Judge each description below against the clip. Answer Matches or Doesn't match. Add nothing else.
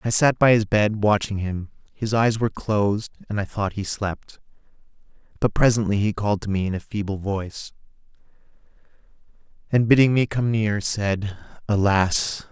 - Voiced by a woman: Doesn't match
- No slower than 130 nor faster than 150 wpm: Doesn't match